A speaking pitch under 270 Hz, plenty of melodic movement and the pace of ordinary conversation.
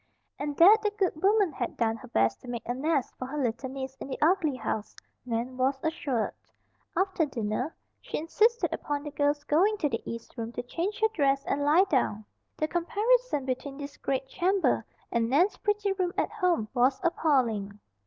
No: very high, 285 Hz; wide, 6.1 semitones; average, 190 wpm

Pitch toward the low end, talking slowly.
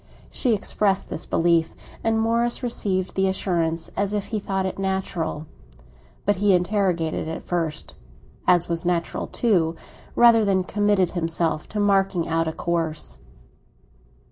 No: medium, 185 Hz; slow, 130 wpm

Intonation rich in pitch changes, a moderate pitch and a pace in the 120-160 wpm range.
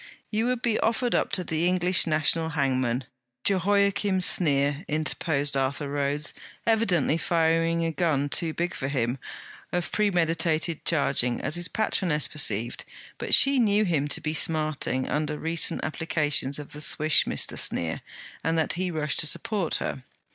No: average, 3.7 semitones; medium, 160 Hz; average, 155 wpm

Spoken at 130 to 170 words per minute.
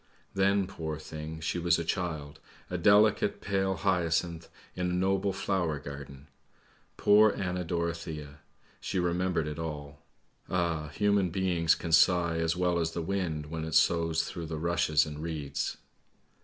Yes: average, 150 wpm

